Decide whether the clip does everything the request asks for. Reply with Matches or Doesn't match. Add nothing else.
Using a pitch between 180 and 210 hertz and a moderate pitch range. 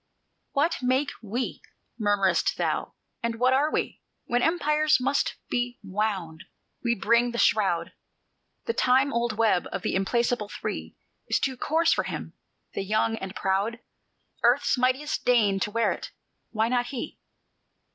Doesn't match